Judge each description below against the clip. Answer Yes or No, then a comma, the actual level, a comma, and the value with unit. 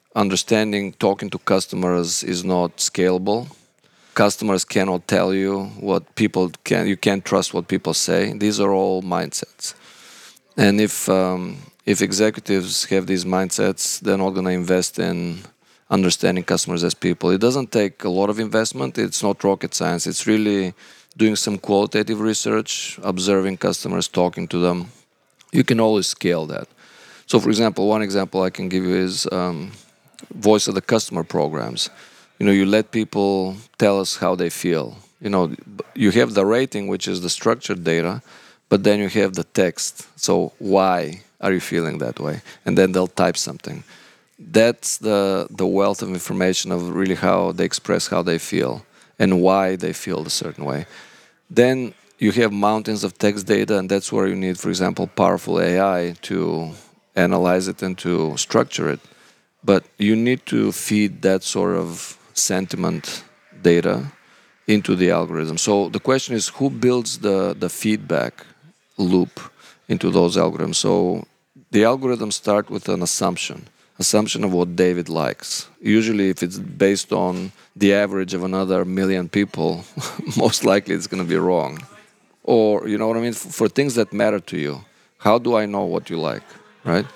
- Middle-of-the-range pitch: No, low, 100 Hz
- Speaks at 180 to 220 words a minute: No, average, 170 wpm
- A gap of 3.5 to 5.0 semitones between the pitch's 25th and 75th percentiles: No, narrow, 2.6 semitones